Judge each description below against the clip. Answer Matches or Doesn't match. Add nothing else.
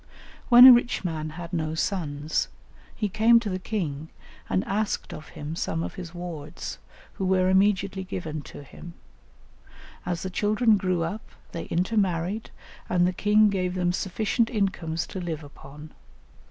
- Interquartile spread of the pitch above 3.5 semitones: Matches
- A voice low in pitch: Doesn't match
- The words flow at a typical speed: Matches